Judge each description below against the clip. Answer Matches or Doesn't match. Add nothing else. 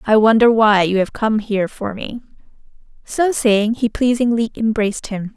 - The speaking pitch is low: Doesn't match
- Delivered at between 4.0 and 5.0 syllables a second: Matches